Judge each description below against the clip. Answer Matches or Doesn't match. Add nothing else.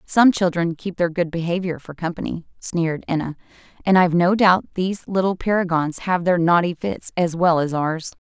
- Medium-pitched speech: Matches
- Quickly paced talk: Doesn't match